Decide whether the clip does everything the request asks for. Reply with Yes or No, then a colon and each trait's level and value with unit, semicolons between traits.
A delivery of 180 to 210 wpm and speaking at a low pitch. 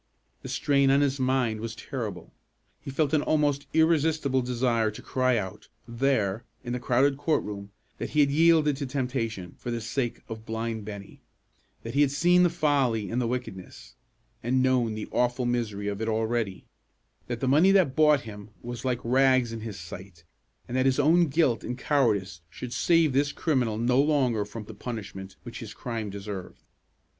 Yes: average, 185 wpm; low, 125 Hz